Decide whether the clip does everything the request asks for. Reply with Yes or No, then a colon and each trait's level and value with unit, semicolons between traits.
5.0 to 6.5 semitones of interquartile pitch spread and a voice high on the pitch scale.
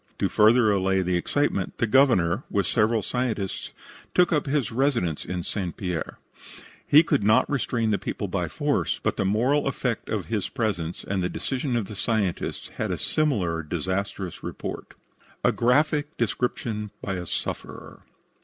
No: average, 5.3 semitones; low, 110 Hz